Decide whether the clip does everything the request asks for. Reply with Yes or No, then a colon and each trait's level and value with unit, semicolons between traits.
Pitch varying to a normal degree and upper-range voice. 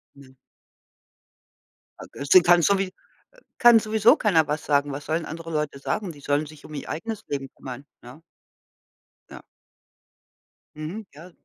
No: average, 4.6 semitones; medium, 155 Hz